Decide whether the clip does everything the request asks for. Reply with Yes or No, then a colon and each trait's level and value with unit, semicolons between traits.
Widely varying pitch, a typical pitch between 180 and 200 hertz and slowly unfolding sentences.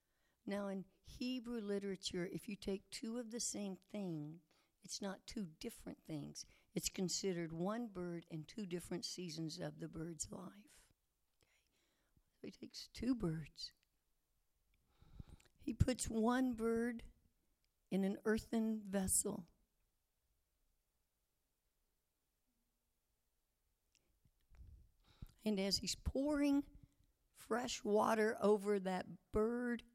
Yes: wide, 6.7 semitones; high, 190 Hz; slow, 105 wpm